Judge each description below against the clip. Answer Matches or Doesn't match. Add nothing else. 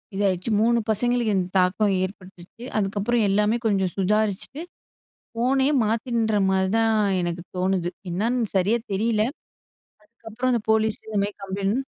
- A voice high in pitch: Matches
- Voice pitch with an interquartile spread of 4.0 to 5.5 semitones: Doesn't match